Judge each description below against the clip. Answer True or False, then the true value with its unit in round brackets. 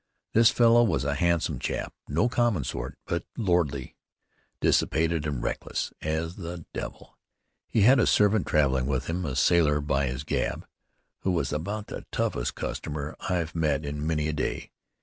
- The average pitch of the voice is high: False (80 Hz)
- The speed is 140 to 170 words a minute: True (165 wpm)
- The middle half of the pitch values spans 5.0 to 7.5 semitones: False (4.1 semitones)